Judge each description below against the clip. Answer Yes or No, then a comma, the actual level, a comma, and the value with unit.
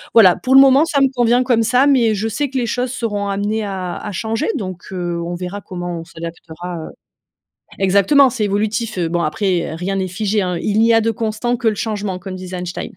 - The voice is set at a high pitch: Yes, high, 205 Hz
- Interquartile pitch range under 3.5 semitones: No, average, 4.2 semitones